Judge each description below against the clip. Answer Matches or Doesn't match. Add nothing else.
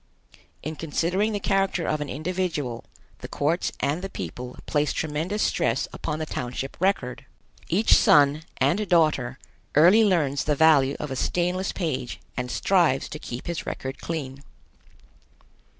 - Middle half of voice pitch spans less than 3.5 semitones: Doesn't match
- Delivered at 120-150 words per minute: Matches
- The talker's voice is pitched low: Doesn't match